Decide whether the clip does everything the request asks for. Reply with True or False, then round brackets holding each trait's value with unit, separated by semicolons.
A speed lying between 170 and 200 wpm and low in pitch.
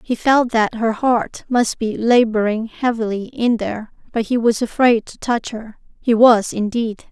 False (175 wpm; 230 Hz)